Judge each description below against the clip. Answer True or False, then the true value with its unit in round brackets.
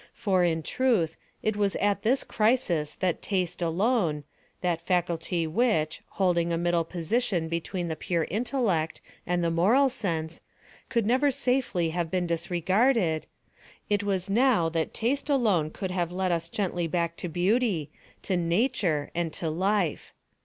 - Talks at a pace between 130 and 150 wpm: True (145 wpm)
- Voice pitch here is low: False (180 Hz)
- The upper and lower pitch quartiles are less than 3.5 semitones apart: False (4.3 semitones)